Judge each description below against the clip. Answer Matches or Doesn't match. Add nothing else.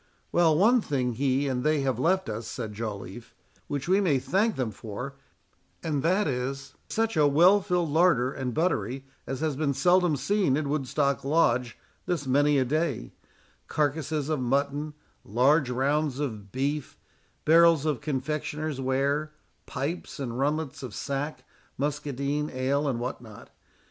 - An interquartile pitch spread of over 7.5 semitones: Doesn't match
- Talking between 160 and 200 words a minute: Doesn't match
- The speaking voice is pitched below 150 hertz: Matches